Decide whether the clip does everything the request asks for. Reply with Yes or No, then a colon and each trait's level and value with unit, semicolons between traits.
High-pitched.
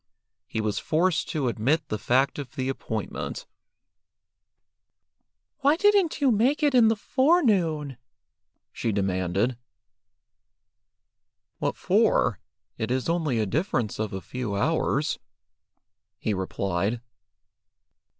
No: low, 135 Hz